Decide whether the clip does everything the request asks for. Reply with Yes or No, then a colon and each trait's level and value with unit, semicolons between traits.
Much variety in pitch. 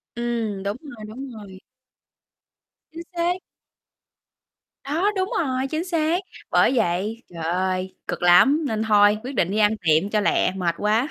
Yes: wide, 6.6 semitones